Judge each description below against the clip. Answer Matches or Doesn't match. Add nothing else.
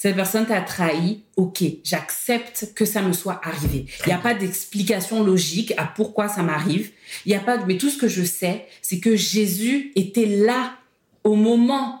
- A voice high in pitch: Matches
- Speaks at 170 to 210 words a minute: Matches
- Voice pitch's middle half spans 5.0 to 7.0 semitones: Doesn't match